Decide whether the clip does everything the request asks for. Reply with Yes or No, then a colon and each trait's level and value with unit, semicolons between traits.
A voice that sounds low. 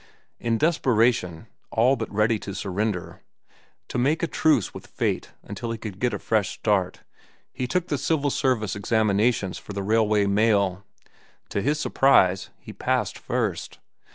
Yes: low, 110 Hz